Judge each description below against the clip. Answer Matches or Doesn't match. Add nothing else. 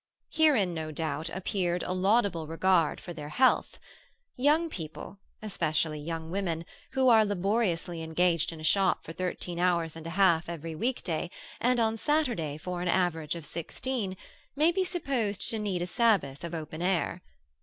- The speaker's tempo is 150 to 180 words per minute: Matches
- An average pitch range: Matches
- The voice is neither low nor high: Matches